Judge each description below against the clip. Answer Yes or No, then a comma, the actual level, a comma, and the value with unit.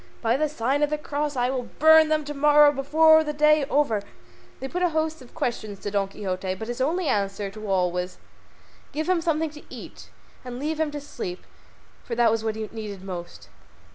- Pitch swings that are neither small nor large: No, wide, 6.1 semitones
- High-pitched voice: Yes, very high, 270 Hz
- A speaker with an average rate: No, fast, 215 wpm